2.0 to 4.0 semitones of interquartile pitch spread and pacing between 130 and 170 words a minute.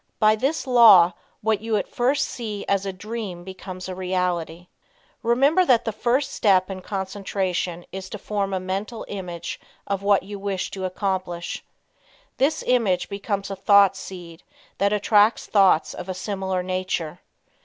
Yes: narrow, 2.5 semitones; average, 155 wpm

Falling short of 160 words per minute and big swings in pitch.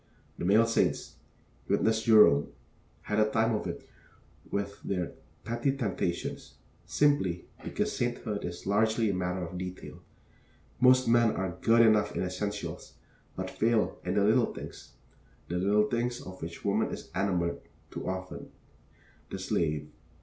No: average, 140 wpm; average, 3.8 semitones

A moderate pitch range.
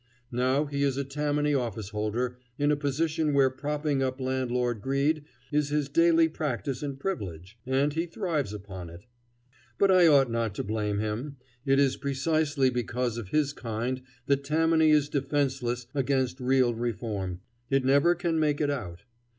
Yes: average, 3.6 semitones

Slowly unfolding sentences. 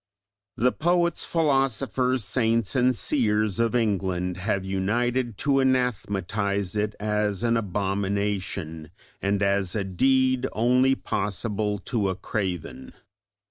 Yes: slow, 110 wpm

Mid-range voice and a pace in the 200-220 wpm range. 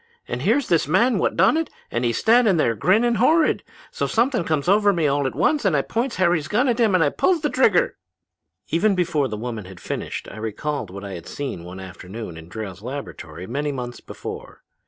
Yes: medium, 150 Hz; fast, 205 wpm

